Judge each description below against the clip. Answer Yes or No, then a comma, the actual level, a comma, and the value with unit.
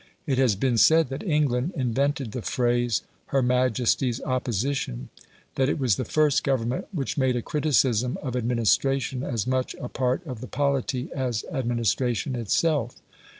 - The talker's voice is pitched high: No, low, 130 Hz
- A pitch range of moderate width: No, narrow, 2.3 semitones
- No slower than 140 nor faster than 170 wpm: Yes, average, 150 wpm